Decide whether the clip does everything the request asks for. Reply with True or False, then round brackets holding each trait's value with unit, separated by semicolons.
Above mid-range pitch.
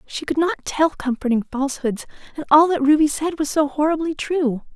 True (295 Hz)